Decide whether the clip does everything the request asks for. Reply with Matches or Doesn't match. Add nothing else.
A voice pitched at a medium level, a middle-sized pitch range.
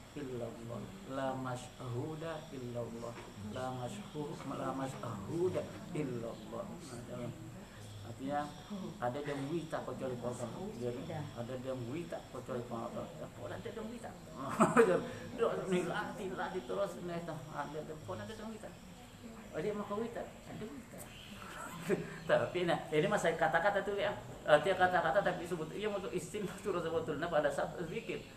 Doesn't match